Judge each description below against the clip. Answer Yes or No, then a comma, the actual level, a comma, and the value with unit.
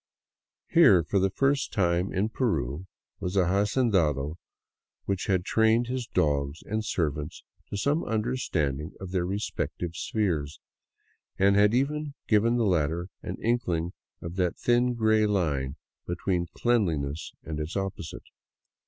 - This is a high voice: No, very low, 95 Hz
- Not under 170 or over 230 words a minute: No, slow, 135 wpm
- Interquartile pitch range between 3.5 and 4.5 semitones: No, average, 5.3 semitones